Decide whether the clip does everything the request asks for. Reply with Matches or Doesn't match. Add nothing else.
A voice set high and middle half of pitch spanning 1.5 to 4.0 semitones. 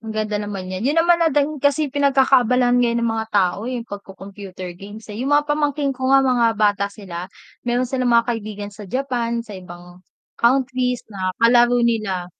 Doesn't match